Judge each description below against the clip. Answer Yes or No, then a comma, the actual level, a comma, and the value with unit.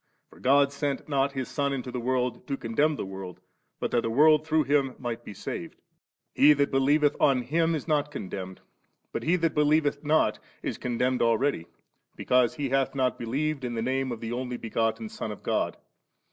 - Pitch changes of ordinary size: Yes, average, 3.6 semitones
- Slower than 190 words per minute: No, average, 200 wpm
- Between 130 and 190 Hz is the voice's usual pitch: Yes, low, 135 Hz